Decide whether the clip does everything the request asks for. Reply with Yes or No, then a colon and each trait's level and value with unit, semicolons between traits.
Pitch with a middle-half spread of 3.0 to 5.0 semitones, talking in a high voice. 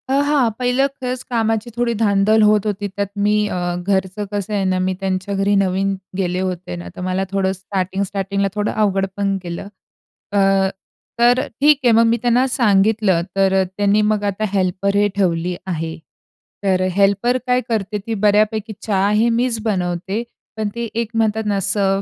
No: narrow, 2.6 semitones; high, 200 Hz